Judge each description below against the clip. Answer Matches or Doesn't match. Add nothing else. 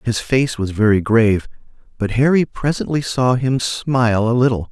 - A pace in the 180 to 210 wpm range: Doesn't match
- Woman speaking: Doesn't match